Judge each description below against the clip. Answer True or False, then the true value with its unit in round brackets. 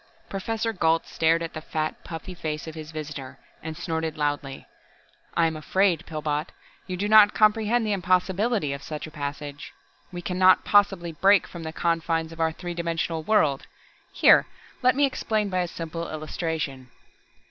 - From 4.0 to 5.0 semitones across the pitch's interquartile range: False (3.4 semitones)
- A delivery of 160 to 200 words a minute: True (170 wpm)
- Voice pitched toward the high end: False (165 Hz)